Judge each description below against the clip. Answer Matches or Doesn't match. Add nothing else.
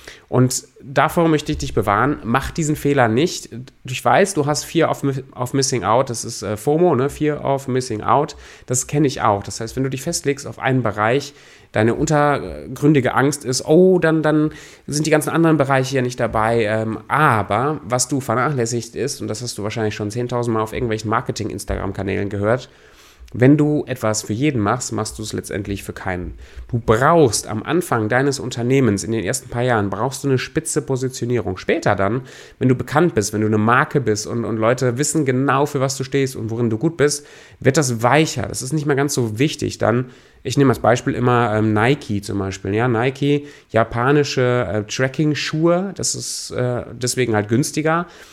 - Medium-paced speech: Doesn't match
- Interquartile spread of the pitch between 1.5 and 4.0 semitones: Doesn't match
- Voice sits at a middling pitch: Doesn't match